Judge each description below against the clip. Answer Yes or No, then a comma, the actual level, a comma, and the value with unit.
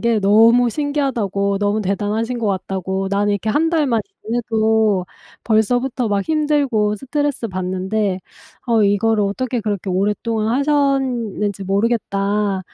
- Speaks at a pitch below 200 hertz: No, high, 215 Hz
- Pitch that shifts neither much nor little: Yes, average, 3.5 semitones